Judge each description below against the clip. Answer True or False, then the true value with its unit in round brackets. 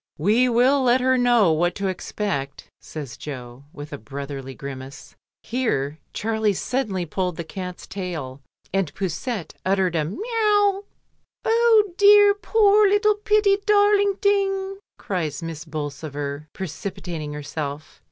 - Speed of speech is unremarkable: False (125 wpm)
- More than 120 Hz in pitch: True (190 Hz)